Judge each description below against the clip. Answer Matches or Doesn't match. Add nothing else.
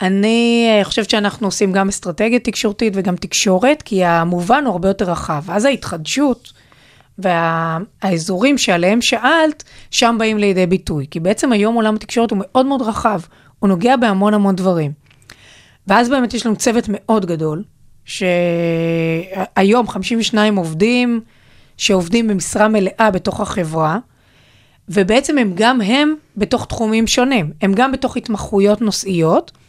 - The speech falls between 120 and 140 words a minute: Matches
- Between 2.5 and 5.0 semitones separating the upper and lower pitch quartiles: Matches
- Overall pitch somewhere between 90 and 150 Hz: Doesn't match